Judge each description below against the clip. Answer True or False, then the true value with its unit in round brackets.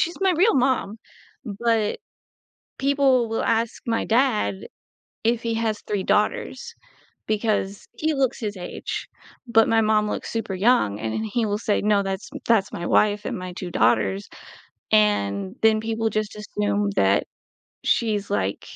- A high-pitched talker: True (215 Hz)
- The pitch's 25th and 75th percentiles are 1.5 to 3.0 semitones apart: False (3.9 semitones)